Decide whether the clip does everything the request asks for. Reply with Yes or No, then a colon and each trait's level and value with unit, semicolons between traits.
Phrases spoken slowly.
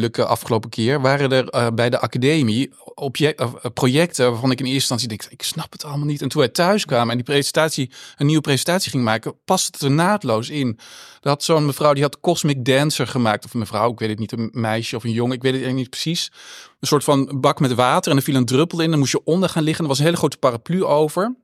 No: fast, 245 wpm